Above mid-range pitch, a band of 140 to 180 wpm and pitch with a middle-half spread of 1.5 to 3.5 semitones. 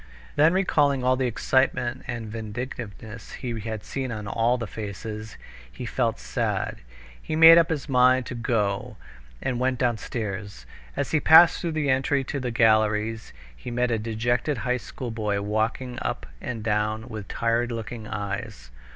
No: low, 115 Hz; average, 160 wpm; average, 3.1 semitones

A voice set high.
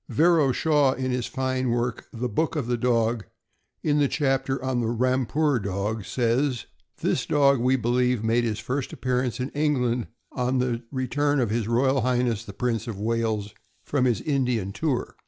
No: low, 125 Hz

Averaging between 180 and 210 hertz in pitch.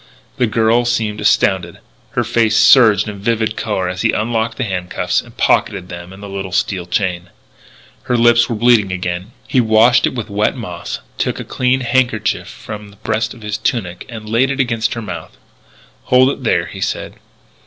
No: low, 110 Hz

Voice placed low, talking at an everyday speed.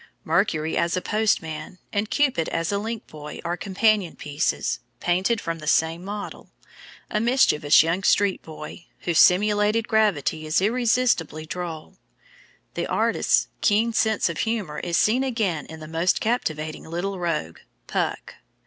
No: medium, 180 Hz; average, 145 wpm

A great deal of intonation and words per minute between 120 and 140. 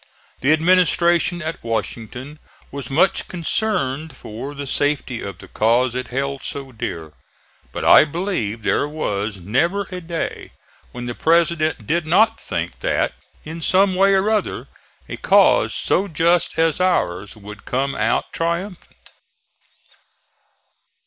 Yes: wide, 6.1 semitones; slow, 135 wpm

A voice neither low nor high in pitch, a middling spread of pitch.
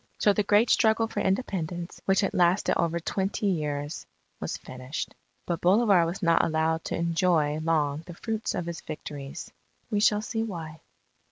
Yes: medium, 170 Hz; average, 4.2 semitones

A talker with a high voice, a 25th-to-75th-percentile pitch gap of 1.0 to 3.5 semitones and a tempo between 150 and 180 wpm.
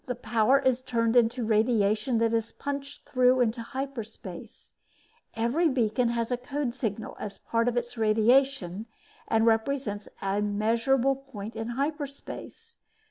No: high, 235 Hz; average, 3.2 semitones; slow, 135 wpm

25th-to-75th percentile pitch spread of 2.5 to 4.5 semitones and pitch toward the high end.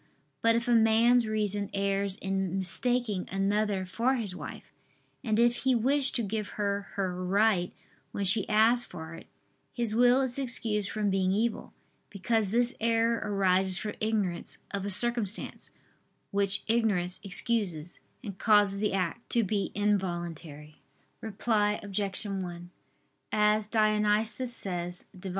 Yes: average, 3.0 semitones; high, 210 Hz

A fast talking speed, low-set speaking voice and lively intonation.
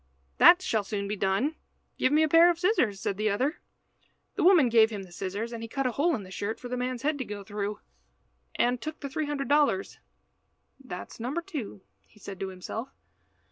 No: fast, 220 wpm; high, 240 Hz; wide, 6.4 semitones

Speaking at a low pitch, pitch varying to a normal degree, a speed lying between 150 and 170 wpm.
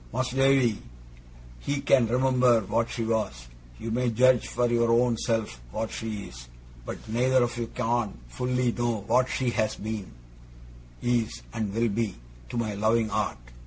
No: low, 115 Hz; narrow, 2.3 semitones; average, 160 wpm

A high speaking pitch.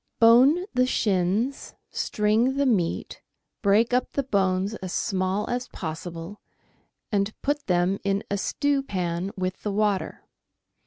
Yes: high, 205 Hz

